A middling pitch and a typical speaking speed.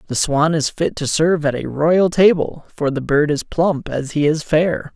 No: medium, 155 Hz; fast, 230 wpm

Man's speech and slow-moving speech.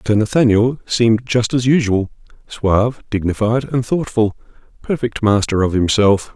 Yes: male; slow, 115 wpm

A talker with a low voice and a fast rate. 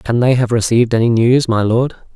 Yes: low, 120 Hz; fast, 225 wpm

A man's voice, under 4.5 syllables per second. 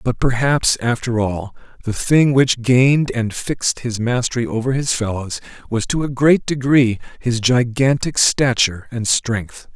Yes: male; 4.3 syllables/s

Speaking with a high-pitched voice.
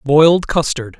No: medium, 150 Hz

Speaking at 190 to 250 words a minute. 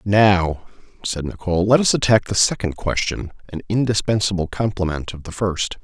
No: average, 155 wpm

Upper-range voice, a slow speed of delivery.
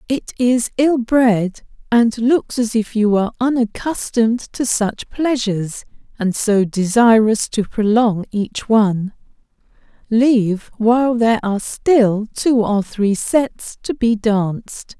Yes: high, 225 Hz; slow, 130 wpm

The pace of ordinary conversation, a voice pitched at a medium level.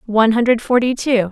No: average, 185 wpm; high, 230 Hz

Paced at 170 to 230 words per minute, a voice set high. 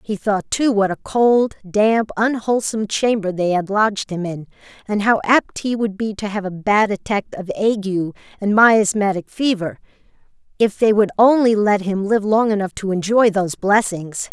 Yes: average, 180 wpm; high, 205 Hz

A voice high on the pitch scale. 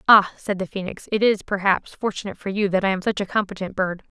Yes: high, 195 Hz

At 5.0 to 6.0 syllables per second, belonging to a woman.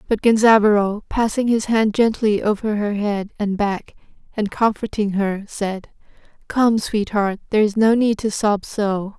No: 4.4 syllables/s; female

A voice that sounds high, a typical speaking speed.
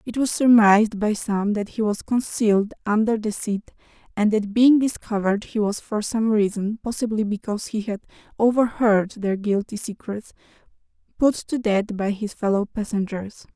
Yes: high, 215 Hz; average, 160 wpm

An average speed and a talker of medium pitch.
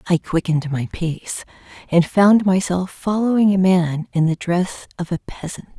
Yes: average, 165 wpm; medium, 180 Hz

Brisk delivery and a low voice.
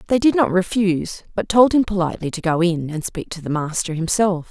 No: fast, 225 wpm; medium, 185 Hz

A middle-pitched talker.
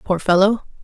No: high, 195 Hz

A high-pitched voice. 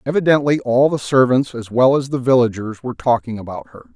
No: low, 125 Hz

